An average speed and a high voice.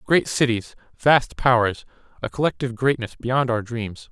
No: average, 145 wpm; low, 120 Hz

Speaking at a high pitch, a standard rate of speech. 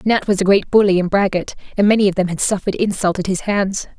No: high, 195 Hz; fast, 255 wpm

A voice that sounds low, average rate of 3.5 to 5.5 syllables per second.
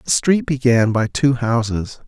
Yes: low, 120 Hz; 4.0 syllables/s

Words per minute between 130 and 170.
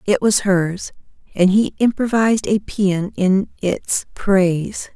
Yes: slow, 135 wpm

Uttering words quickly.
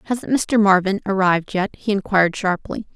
No: average, 165 wpm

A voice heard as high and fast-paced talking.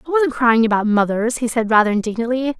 Yes: high, 240 Hz; fast, 210 wpm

